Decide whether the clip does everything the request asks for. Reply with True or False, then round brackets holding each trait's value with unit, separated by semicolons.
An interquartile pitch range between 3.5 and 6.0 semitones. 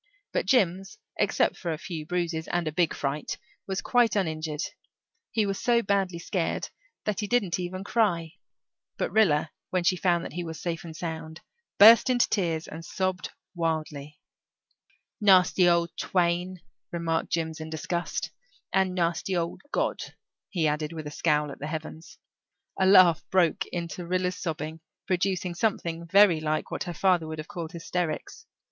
False (2.7 semitones)